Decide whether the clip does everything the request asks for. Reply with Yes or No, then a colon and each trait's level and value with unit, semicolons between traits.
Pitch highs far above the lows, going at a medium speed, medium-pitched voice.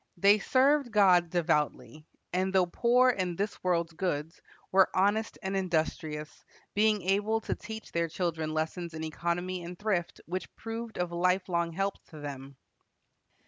No: average, 3.3 semitones; average, 145 wpm; medium, 180 Hz